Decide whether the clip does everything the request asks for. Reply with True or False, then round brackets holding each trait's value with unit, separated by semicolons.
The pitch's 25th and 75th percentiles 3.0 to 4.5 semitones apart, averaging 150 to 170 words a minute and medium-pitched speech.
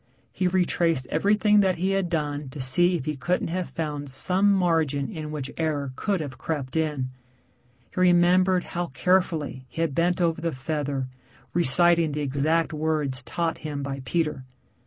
True (3.6 semitones; 165 wpm; 160 Hz)